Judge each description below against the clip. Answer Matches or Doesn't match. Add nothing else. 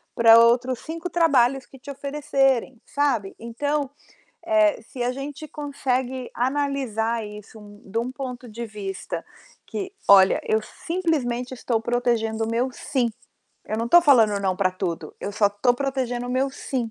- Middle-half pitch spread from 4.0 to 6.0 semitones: Doesn't match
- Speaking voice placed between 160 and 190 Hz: Doesn't match